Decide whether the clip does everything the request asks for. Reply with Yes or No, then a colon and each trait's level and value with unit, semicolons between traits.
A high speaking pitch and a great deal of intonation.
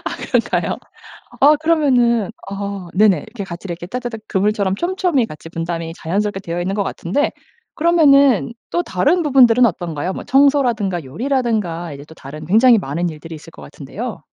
Yes: high, 200 Hz; wide, 7.1 semitones